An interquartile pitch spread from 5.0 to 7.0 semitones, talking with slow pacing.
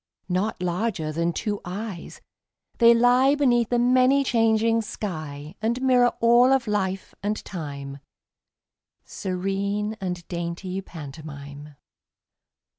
Yes: wide, 5.5 semitones; slow, 110 wpm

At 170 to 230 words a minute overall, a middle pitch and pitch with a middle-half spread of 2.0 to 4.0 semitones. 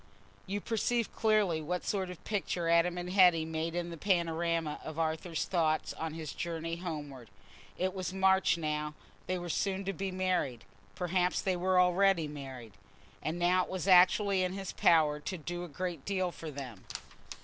Yes: average, 175 wpm; medium, 175 Hz; average, 2.7 semitones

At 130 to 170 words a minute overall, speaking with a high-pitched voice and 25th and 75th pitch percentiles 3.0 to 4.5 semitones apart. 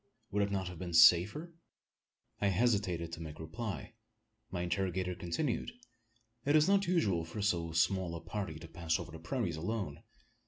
No: average, 165 wpm; very low, 90 Hz; average, 4.2 semitones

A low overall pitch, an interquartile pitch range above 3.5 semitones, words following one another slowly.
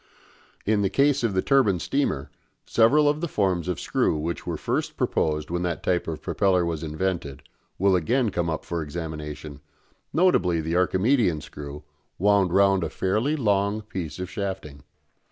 No: very low, 95 Hz; average, 4.3 semitones; average, 165 wpm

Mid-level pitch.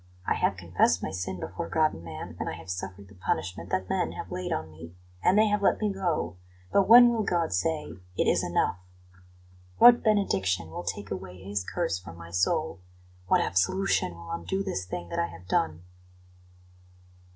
No: very low, 95 Hz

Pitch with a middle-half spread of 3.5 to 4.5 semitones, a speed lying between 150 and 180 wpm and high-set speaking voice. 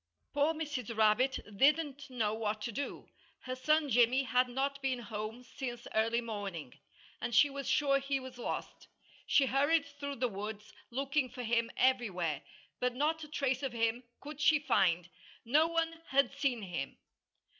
Yes: average, 3.9 semitones; average, 165 wpm; very high, 255 Hz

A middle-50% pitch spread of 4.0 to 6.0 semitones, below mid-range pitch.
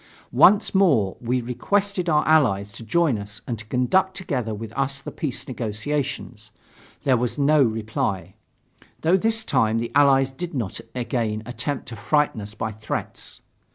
Yes: average, 5.3 semitones; low, 125 Hz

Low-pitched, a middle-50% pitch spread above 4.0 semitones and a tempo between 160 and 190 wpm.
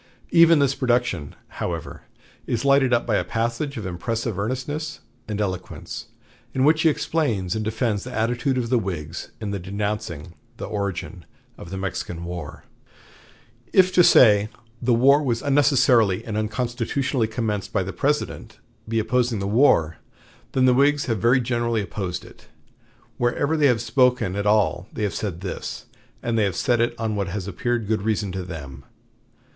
Yes: low, 115 Hz; average, 4.4 semitones; average, 165 wpm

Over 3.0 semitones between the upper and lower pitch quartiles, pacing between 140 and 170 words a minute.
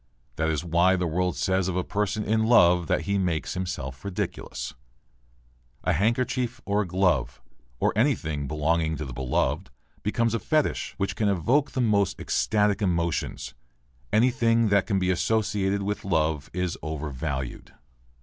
Yes: average, 4.7 semitones; average, 150 wpm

